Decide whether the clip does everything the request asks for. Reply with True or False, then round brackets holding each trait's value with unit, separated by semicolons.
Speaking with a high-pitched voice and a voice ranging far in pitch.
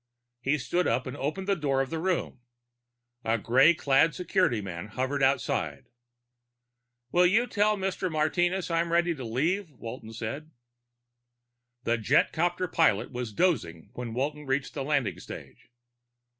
False (145 Hz; 5.9 semitones)